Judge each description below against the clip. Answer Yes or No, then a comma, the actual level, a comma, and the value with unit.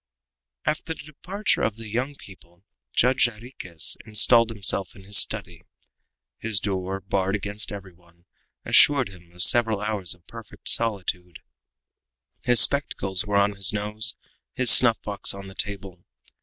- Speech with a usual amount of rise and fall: Yes, average, 3.3 semitones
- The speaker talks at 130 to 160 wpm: Yes, average, 145 wpm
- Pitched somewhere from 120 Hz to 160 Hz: No, low, 100 Hz